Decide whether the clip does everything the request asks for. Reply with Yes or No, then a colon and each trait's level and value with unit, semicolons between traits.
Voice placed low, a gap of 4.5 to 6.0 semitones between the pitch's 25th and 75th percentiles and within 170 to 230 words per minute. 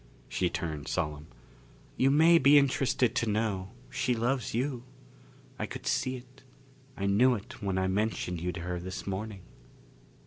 No: low, 105 Hz; wide, 5.5 semitones; average, 160 wpm